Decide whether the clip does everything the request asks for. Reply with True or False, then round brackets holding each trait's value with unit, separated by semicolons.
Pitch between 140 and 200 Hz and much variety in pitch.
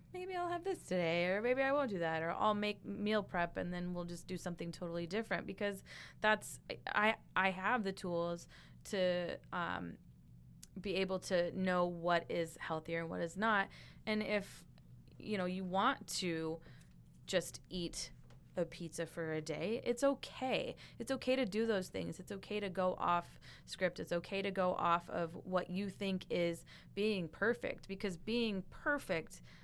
False (185 Hz; 3.6 semitones)